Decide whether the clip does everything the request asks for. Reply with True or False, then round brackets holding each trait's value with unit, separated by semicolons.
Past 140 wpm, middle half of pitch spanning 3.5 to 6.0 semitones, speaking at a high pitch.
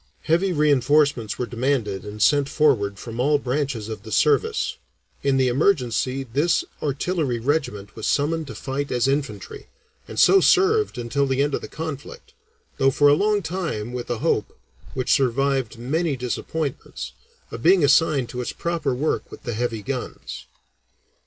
False (160 wpm; 4.1 semitones; 135 Hz)